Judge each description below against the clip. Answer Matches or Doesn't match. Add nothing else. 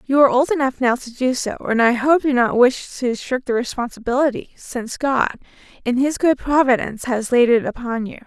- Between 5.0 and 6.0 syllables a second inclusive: Matches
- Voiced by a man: Doesn't match